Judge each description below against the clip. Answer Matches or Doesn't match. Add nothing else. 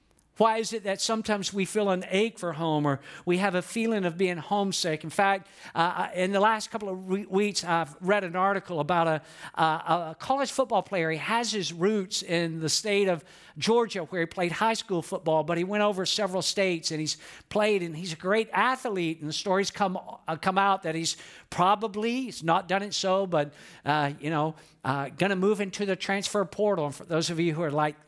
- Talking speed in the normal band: Doesn't match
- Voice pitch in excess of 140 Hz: Matches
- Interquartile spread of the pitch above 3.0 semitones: Matches